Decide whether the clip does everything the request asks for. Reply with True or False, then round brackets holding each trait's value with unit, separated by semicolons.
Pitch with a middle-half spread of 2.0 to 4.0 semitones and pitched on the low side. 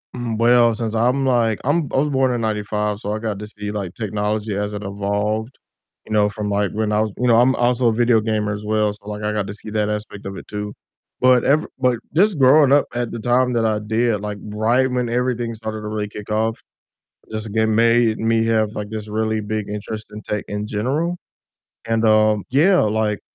True (2.4 semitones; 110 Hz)